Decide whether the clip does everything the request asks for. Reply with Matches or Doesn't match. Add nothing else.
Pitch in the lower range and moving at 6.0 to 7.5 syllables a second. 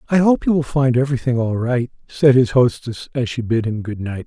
Doesn't match